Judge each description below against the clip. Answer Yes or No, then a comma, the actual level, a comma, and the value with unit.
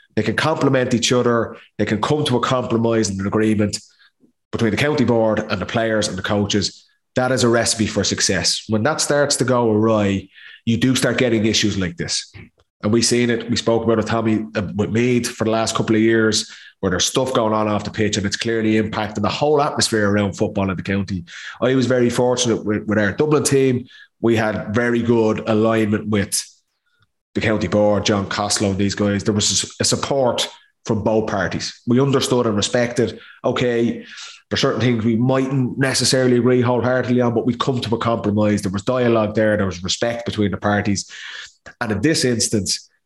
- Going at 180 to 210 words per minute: Yes, average, 200 wpm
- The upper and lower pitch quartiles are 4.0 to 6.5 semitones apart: No, average, 2.7 semitones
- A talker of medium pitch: No, low, 110 Hz